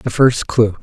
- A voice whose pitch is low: Yes, low, 115 Hz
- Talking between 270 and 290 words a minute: No, fast, 220 wpm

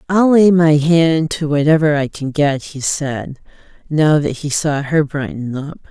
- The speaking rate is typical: Yes, average, 185 wpm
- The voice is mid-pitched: Yes, medium, 150 Hz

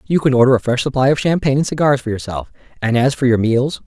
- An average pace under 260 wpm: No, fast, 265 wpm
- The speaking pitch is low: Yes, low, 130 Hz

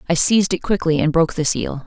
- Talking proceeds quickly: Yes, fast, 260 wpm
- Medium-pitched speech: Yes, medium, 170 Hz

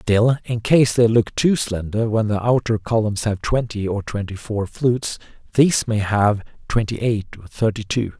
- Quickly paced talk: No, average, 185 wpm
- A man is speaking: Yes, male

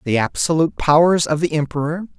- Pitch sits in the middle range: Yes, medium, 150 Hz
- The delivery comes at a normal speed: Yes, average, 165 wpm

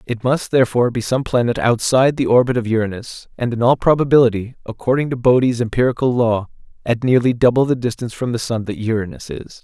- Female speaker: No, male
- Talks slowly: No, average, 195 wpm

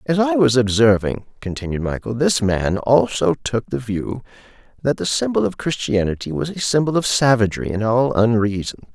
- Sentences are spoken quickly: No, average, 170 wpm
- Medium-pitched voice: No, low, 120 Hz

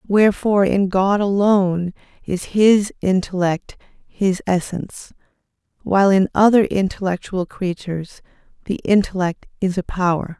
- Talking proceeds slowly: Yes, slow, 110 wpm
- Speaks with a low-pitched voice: No, high, 190 Hz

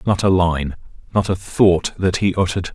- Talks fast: No, average, 195 wpm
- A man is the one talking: Yes, male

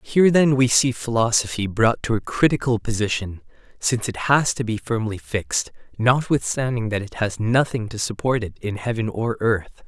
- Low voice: Yes, low, 115 Hz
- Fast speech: No, average, 175 wpm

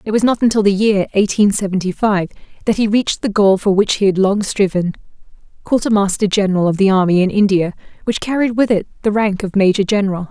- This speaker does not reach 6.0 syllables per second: No, 6.2 syllables/s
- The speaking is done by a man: No, female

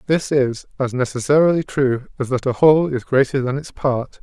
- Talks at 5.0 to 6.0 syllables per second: Yes, 5.3 syllables/s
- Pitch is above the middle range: No, low, 135 Hz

